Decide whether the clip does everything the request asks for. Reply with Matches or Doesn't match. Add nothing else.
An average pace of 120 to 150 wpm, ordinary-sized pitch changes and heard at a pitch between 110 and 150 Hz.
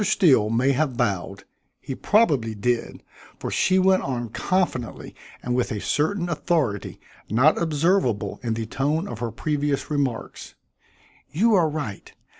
Doesn't match